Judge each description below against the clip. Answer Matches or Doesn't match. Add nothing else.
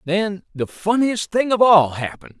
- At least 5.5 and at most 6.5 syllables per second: Doesn't match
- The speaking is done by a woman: Doesn't match